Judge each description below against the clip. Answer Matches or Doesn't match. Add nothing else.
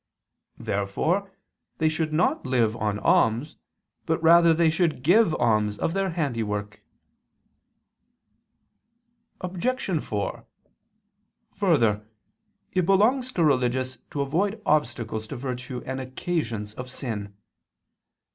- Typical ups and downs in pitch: Doesn't match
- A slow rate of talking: Matches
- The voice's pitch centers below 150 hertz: Matches